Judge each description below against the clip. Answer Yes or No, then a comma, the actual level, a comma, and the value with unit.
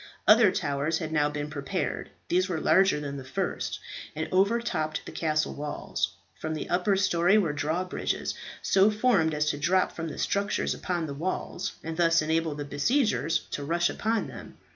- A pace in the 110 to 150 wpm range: No, average, 175 wpm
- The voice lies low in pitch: No, medium, 165 Hz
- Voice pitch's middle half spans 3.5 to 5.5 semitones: Yes, average, 4.0 semitones